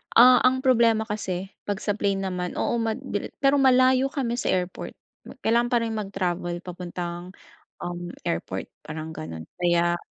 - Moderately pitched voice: No, high, 195 Hz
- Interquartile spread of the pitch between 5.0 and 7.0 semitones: Yes, average, 5.3 semitones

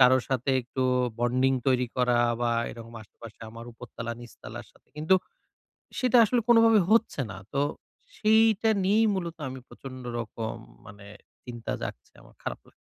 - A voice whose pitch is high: No, low, 130 Hz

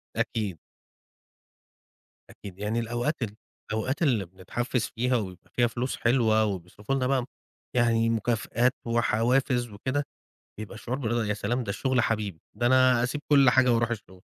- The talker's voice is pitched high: No, low, 120 Hz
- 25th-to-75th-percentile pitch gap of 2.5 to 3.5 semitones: Yes, average, 2.9 semitones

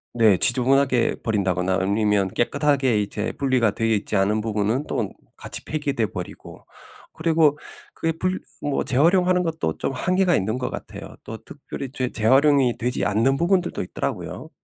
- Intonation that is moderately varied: No, wide, 5.8 semitones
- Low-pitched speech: Yes, low, 125 Hz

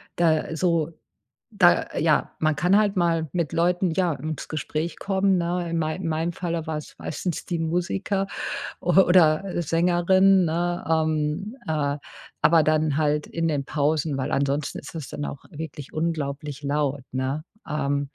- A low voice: No, medium, 160 Hz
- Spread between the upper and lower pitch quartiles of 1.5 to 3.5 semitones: Yes, narrow, 2.5 semitones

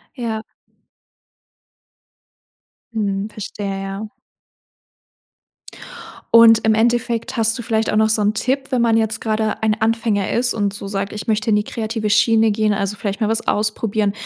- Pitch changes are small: Yes, narrow, 1.4 semitones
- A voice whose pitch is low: No, high, 220 Hz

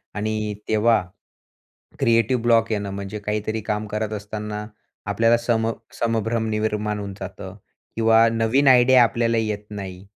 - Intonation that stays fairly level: Yes, narrow, 1.6 semitones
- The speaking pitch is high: No, low, 110 Hz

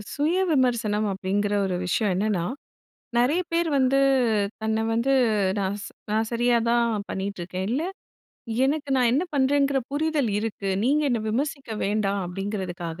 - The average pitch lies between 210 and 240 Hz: Yes, high, 225 Hz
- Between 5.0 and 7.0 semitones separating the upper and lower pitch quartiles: Yes, wide, 5.4 semitones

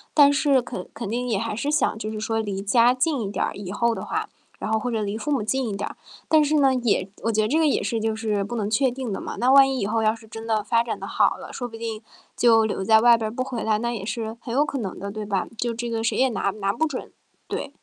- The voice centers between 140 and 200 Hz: No, high, 230 Hz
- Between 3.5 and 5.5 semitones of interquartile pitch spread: No, average, 2.8 semitones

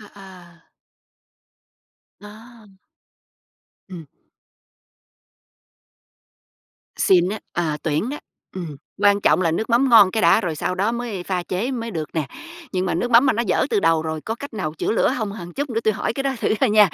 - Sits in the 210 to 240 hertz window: No, high, 200 Hz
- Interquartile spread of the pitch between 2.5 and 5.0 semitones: Yes, average, 4.7 semitones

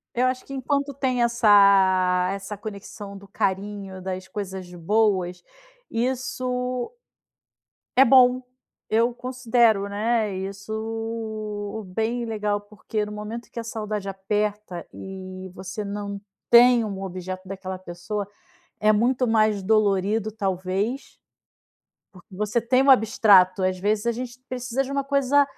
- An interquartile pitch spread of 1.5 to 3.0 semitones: No, average, 3.6 semitones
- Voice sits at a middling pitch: No, high, 210 Hz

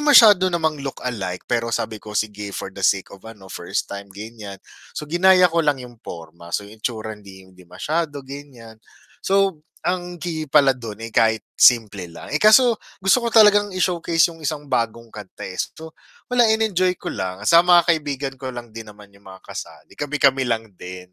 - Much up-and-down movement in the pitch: Yes, wide, 8.3 semitones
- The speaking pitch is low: Yes, low, 125 Hz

